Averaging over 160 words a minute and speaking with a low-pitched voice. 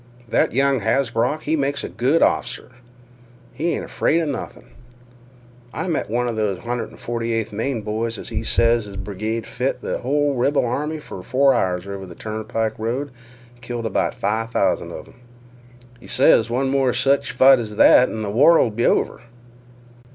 Yes: average, 180 wpm; low, 120 Hz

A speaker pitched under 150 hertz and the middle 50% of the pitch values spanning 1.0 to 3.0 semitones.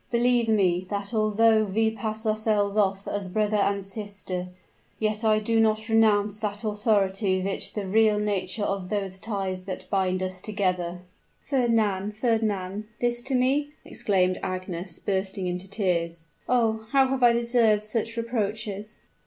No: high, 210 Hz; average, 2.7 semitones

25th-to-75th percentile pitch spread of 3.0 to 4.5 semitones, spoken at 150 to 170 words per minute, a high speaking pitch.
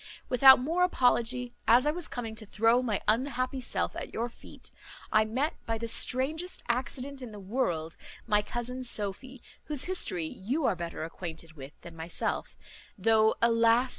Yes: average, 3.8 semitones; average, 165 wpm; high, 235 Hz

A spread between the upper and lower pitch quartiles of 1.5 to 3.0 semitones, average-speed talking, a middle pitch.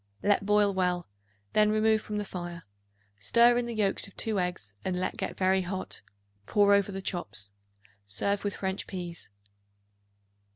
No: narrow, 2.6 semitones; average, 160 wpm; high, 195 Hz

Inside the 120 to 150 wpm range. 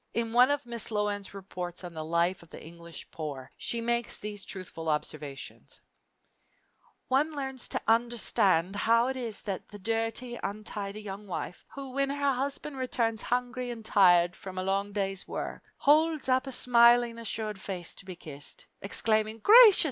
No: average, 165 wpm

